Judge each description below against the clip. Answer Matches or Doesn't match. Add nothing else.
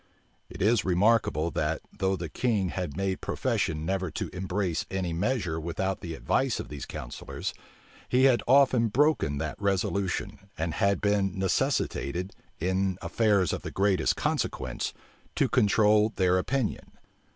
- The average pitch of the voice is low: Matches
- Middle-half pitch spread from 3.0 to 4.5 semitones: Matches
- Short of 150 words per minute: Matches